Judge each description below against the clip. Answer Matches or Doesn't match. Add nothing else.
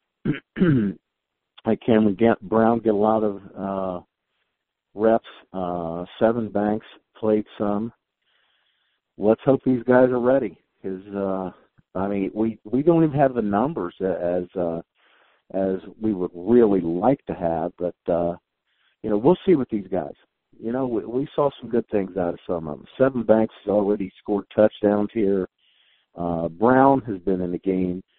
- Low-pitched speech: Matches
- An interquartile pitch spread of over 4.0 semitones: Doesn't match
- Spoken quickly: Doesn't match